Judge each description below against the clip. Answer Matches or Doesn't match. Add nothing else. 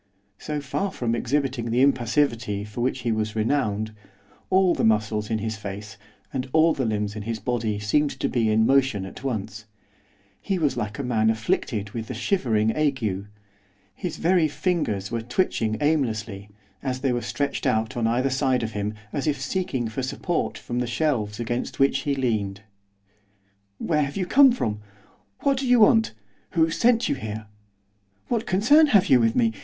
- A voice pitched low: Matches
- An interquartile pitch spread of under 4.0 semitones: Doesn't match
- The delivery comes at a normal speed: Matches